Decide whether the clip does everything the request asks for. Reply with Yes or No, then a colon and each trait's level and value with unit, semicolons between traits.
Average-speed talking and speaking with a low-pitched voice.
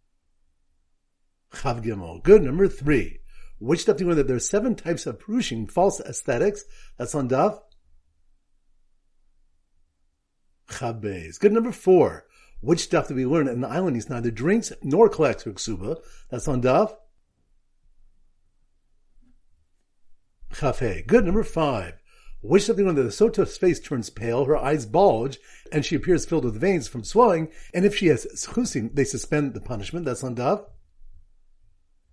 Yes: average, 145 wpm; low, 130 Hz